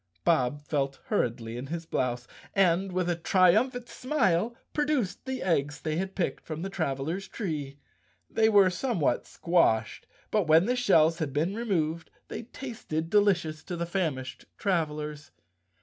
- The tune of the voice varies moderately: Yes, average, 4.9 semitones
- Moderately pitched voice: Yes, medium, 170 Hz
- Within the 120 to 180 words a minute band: Yes, average, 150 wpm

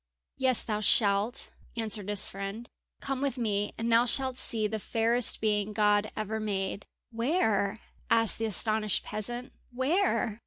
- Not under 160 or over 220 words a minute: No, average, 145 wpm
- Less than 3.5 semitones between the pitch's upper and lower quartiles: Yes, narrow, 2.5 semitones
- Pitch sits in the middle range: No, high, 220 Hz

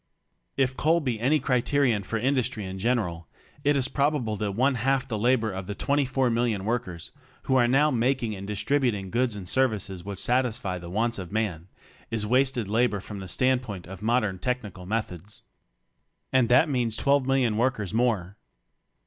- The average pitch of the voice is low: Yes, low, 115 Hz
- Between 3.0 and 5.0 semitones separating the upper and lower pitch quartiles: Yes, average, 4.4 semitones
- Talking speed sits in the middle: Yes, average, 175 wpm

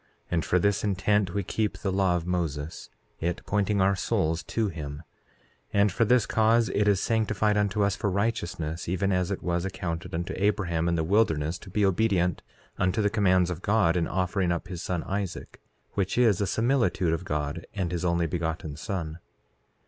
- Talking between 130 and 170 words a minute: No, average, 185 wpm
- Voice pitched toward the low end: Yes, very low, 95 Hz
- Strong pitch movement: No, average, 3.2 semitones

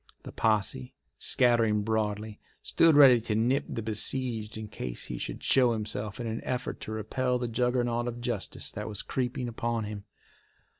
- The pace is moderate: Yes, average, 165 wpm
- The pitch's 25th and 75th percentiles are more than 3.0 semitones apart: No, narrow, 2.4 semitones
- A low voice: Yes, low, 115 Hz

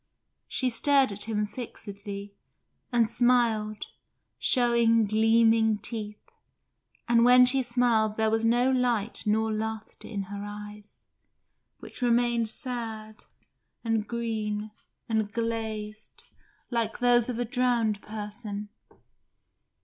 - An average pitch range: No, narrow, 2.2 semitones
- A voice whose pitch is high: Yes, high, 225 Hz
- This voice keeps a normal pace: No, slow, 110 wpm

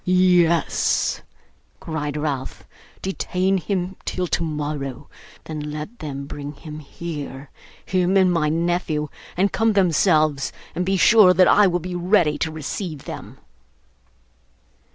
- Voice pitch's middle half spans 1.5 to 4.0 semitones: Yes, average, 3.4 semitones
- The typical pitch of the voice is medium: Yes, medium, 170 Hz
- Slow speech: Yes, slow, 125 wpm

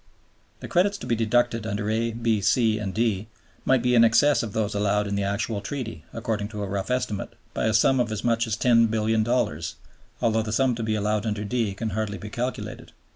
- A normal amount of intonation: No, narrow, 2.2 semitones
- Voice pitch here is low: Yes, low, 110 Hz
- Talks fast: Yes, fast, 215 wpm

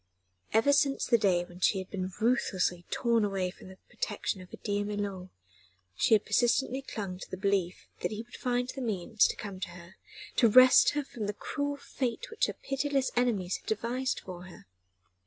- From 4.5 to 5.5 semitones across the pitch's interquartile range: Yes, average, 4.8 semitones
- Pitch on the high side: Yes, high, 210 Hz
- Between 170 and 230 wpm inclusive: Yes, average, 195 wpm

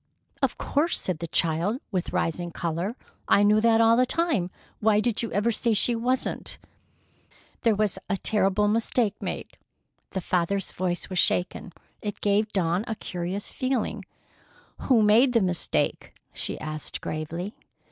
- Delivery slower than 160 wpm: Yes, average, 150 wpm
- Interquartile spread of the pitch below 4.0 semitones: No, average, 4.3 semitones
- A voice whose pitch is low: No, high, 205 Hz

